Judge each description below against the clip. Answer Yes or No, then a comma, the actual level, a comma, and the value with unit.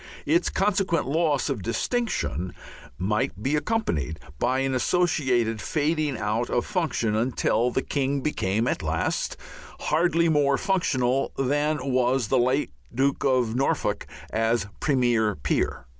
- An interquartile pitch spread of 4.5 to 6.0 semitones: Yes, average, 5.1 semitones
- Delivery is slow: Yes, slow, 130 wpm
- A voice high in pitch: No, low, 130 Hz